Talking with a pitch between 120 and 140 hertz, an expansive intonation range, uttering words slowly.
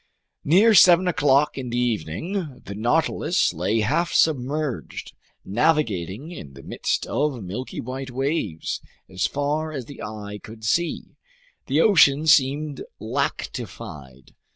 Yes: low, 135 Hz; wide, 6.2 semitones; slow, 125 wpm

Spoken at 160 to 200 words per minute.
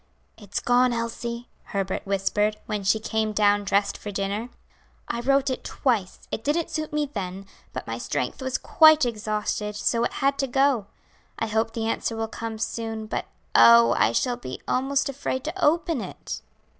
Yes: average, 175 wpm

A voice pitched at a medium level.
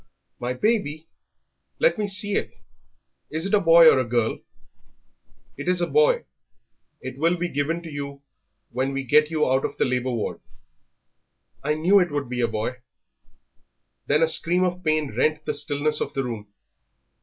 Yes: medium, 150 Hz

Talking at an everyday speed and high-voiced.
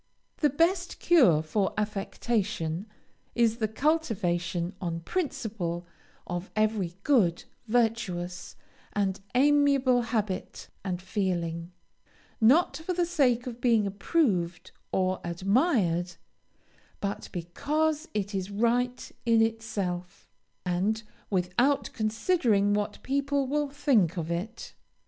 No: slow, 105 wpm; high, 215 Hz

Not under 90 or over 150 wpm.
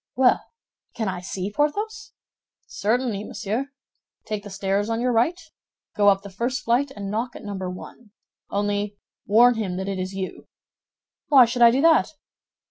No: average, 165 wpm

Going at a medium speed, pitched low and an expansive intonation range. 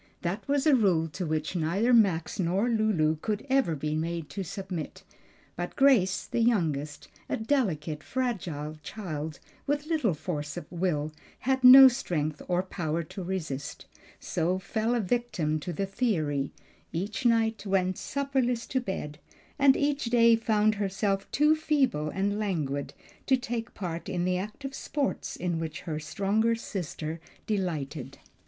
No: average, 150 wpm; high, 190 Hz; wide, 6.6 semitones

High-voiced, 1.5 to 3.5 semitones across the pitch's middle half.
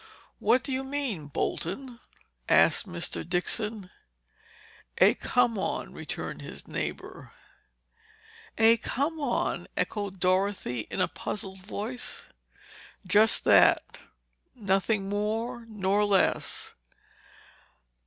No: high, 210 Hz; average, 3.9 semitones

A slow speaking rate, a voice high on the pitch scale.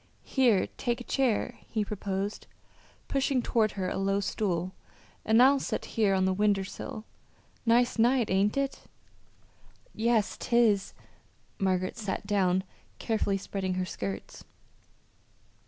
Yes: slow, 125 wpm; high, 210 Hz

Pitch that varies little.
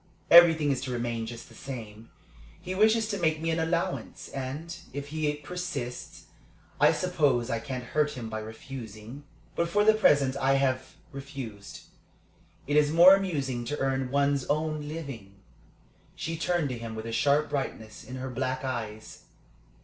No: average, 4.7 semitones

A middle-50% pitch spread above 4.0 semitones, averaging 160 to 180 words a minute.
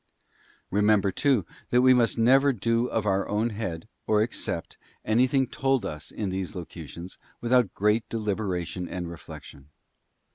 No: average, 4.4 semitones; average, 140 wpm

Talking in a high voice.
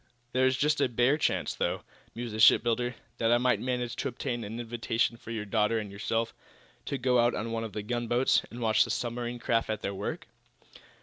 No: low, 120 Hz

